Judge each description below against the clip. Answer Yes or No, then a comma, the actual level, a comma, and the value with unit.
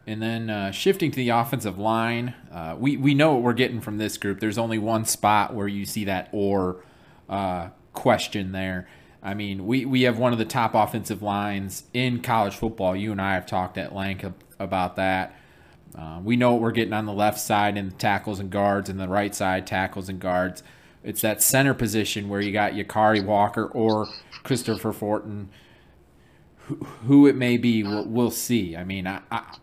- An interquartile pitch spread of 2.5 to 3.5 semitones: Yes, average, 2.9 semitones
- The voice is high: No, low, 105 Hz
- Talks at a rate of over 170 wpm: Yes, fast, 205 wpm